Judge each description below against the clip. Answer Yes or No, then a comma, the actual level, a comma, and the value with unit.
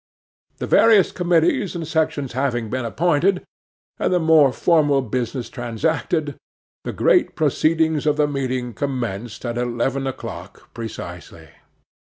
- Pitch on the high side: No, medium, 140 Hz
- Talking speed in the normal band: No, slow, 125 wpm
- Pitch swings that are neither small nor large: Yes, average, 4.7 semitones